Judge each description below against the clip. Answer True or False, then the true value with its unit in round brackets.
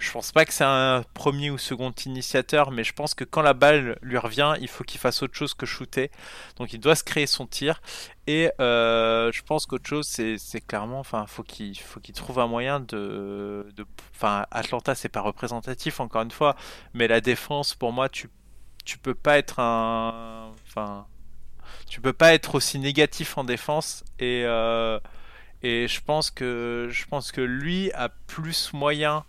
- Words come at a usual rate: True (190 wpm)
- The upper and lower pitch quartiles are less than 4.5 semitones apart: True (4.0 semitones)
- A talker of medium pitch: False (130 Hz)